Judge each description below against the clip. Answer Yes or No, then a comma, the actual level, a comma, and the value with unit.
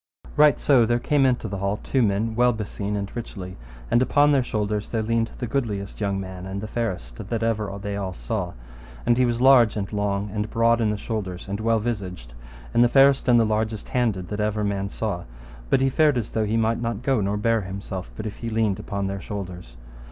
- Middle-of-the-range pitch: No, low, 110 Hz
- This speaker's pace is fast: Yes, fast, 220 wpm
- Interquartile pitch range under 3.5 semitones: Yes, average, 2.9 semitones